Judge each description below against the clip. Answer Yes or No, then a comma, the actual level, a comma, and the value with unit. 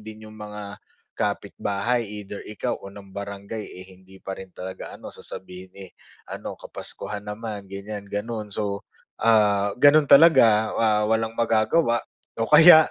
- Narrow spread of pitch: Yes, narrow, 2.1 semitones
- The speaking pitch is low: Yes, low, 105 Hz